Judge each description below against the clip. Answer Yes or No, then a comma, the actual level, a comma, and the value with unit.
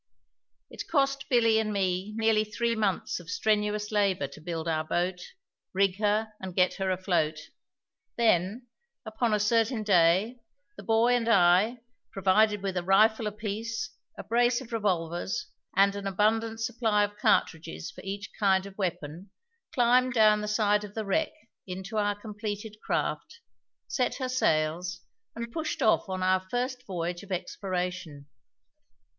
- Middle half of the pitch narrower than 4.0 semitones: Yes, average, 3.3 semitones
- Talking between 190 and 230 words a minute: No, average, 150 wpm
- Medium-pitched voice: No, high, 205 Hz